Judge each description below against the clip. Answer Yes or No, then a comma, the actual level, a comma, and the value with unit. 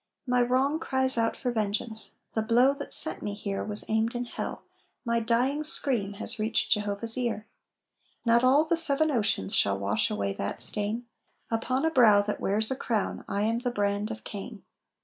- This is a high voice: Yes, high, 225 Hz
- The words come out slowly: No, average, 185 wpm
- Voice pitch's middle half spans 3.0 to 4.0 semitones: Yes, average, 3.4 semitones